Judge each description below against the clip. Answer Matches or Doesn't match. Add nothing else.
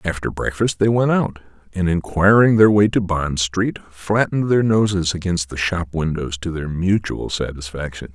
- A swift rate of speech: Doesn't match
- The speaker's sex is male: Matches